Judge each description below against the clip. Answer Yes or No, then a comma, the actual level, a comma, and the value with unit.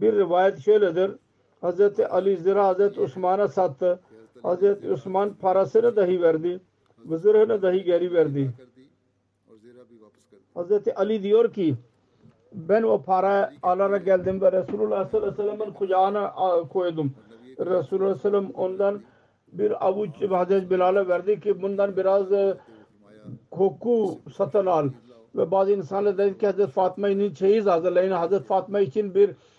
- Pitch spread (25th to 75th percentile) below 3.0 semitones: Yes, narrow, 2.4 semitones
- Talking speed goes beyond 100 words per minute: Yes, average, 130 wpm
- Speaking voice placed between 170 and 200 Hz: Yes, high, 190 Hz